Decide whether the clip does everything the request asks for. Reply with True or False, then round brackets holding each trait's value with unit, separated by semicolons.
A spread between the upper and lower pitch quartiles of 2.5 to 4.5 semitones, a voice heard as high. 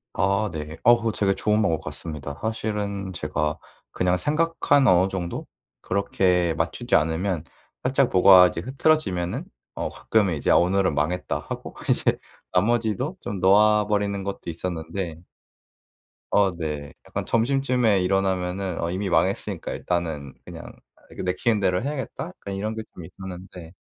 False (3.6 semitones; 95 Hz)